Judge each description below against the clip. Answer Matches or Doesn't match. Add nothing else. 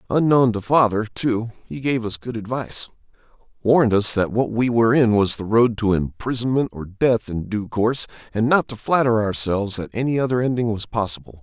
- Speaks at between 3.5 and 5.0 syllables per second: Doesn't match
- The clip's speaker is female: Doesn't match